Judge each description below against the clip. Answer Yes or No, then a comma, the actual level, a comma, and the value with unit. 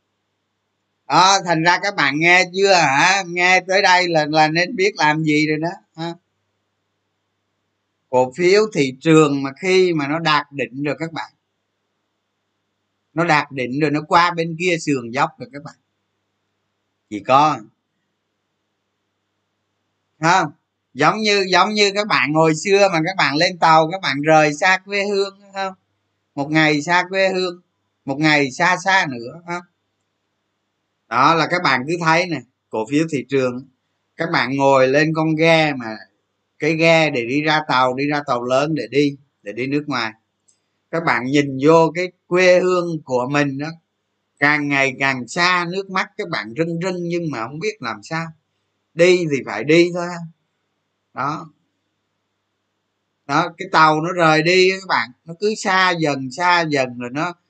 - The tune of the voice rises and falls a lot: Yes, wide, 8.1 semitones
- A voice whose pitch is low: No, medium, 150 Hz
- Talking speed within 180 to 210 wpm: No, average, 170 wpm